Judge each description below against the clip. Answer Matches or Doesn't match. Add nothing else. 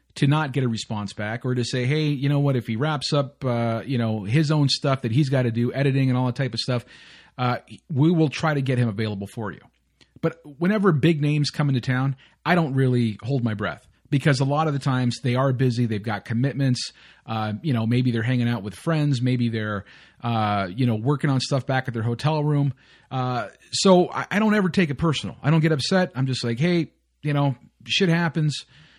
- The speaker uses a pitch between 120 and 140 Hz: Matches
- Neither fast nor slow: Doesn't match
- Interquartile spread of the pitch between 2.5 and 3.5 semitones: Doesn't match